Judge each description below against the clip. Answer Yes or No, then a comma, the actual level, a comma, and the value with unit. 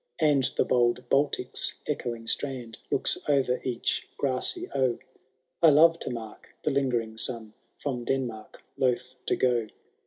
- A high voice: No, low, 125 Hz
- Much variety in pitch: No, average, 2.7 semitones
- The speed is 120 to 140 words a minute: Yes, slow, 135 wpm